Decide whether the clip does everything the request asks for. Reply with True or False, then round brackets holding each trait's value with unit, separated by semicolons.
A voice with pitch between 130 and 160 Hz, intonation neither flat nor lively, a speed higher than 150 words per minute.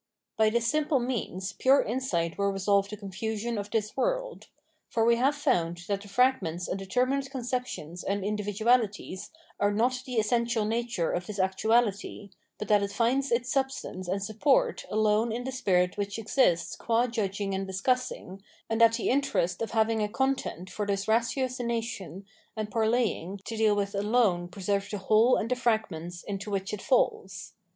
False (215 Hz; 3.6 semitones; 170 wpm)